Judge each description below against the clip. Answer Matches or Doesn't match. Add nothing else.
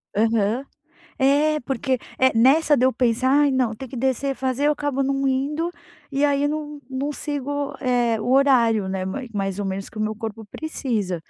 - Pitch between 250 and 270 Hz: Matches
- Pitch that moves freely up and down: Doesn't match